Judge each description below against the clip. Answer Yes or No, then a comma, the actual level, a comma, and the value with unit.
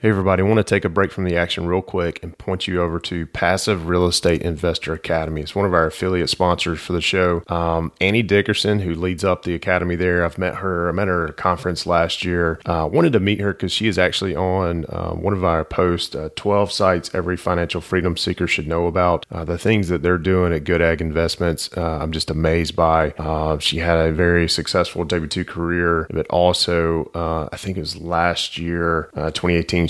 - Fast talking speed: Yes, fast, 225 wpm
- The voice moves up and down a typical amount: No, narrow, 1.8 semitones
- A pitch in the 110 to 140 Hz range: No, very low, 85 Hz